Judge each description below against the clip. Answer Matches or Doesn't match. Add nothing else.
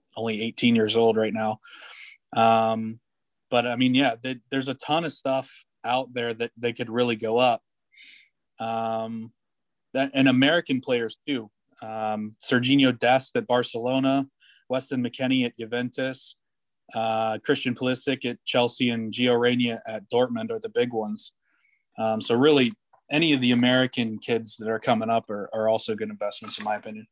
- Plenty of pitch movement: Doesn't match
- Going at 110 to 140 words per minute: Doesn't match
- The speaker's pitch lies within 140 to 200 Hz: Doesn't match